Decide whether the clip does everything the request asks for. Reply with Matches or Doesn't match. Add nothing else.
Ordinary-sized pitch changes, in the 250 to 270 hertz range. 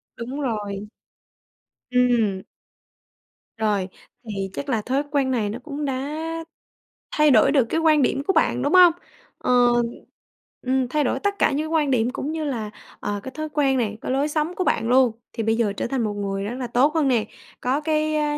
Matches